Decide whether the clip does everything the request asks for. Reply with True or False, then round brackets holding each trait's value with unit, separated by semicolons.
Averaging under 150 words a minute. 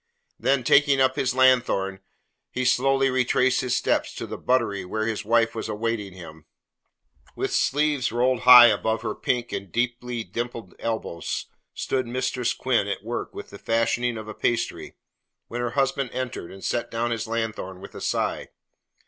False (165 wpm)